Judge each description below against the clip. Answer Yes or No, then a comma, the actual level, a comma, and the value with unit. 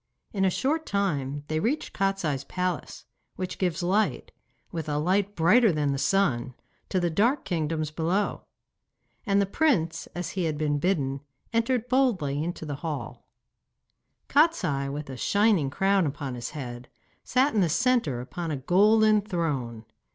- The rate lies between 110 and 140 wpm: No, average, 155 wpm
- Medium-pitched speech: Yes, medium, 175 Hz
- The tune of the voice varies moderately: No, wide, 5.7 semitones